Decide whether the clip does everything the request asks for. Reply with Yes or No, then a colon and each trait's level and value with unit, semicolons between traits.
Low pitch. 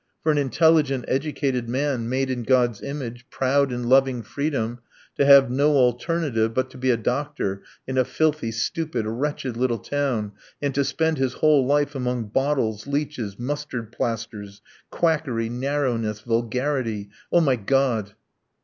Yes: low, 130 Hz